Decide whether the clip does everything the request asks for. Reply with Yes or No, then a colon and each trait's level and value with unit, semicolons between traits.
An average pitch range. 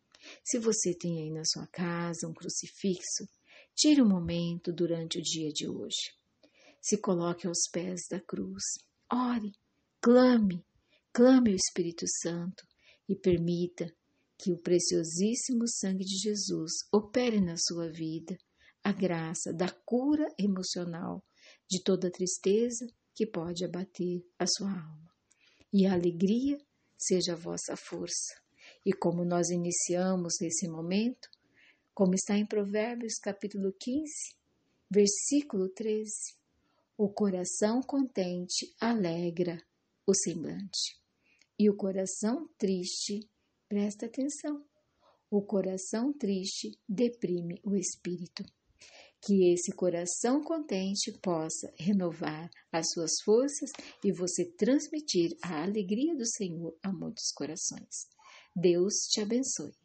Yes: average, 3.9 semitones